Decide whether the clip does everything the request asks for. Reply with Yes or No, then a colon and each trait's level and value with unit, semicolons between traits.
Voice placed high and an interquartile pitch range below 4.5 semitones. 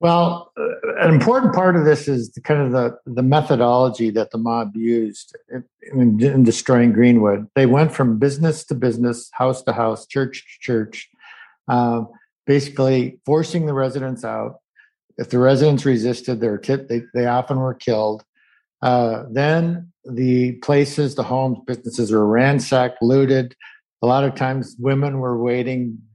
No: low, 125 Hz; average, 2.8 semitones